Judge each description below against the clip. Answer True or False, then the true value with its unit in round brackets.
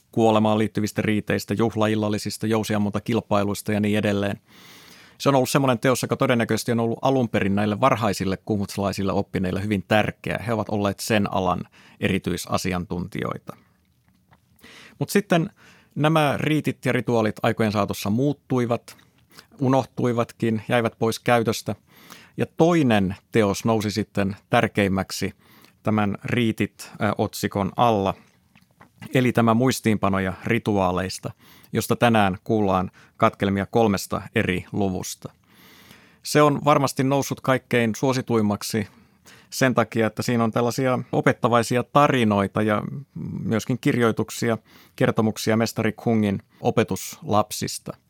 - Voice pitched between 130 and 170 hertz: False (110 Hz)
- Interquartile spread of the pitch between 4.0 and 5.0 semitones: False (3.2 semitones)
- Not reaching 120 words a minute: True (105 wpm)